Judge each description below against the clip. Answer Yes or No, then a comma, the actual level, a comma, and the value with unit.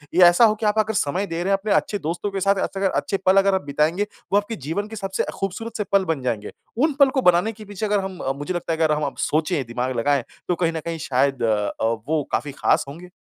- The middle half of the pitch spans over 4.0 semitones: Yes, wide, 5.4 semitones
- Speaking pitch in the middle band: Yes, medium, 180 Hz